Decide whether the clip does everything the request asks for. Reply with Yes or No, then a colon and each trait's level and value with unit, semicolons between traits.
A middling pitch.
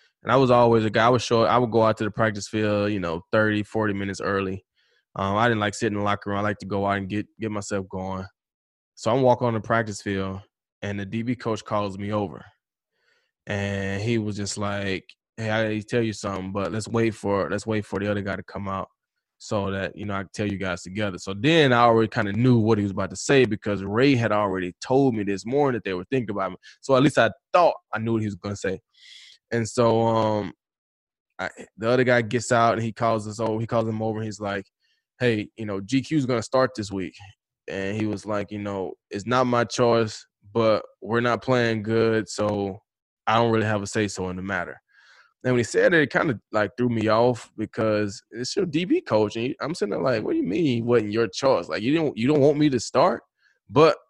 No: low, 110 Hz